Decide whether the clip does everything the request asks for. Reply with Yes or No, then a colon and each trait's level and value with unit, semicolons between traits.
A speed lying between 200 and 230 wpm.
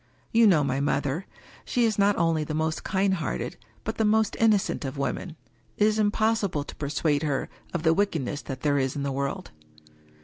Yes: fast, 205 wpm